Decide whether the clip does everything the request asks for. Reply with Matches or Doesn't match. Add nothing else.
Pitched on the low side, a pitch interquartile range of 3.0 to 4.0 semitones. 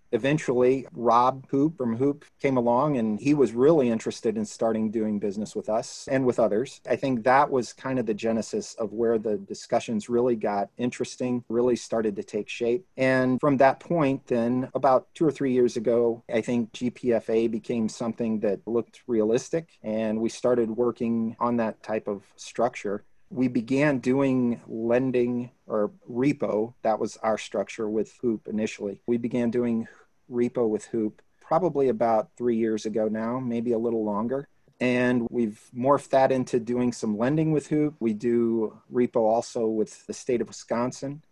Doesn't match